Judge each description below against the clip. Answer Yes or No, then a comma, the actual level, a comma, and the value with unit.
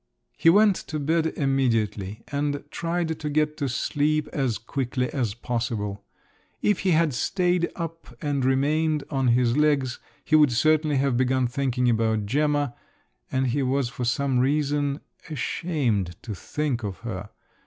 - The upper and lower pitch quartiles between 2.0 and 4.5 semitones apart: Yes, average, 4.0 semitones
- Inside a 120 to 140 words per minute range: No, average, 150 wpm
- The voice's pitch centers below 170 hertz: Yes, medium, 140 Hz